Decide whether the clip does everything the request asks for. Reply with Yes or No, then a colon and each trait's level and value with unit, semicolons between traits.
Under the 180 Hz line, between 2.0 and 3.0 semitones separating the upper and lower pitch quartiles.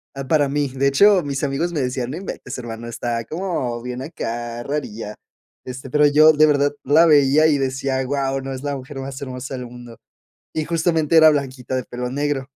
Yes: low, 135 Hz; average, 2.7 semitones